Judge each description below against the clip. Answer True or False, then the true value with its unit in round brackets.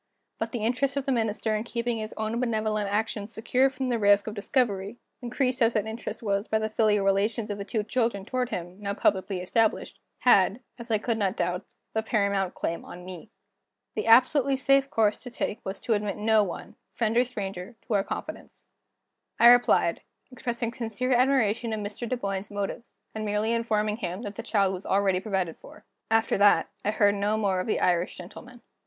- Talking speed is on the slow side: False (195 wpm)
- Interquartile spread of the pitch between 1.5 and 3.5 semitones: True (2.8 semitones)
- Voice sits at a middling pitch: False (215 Hz)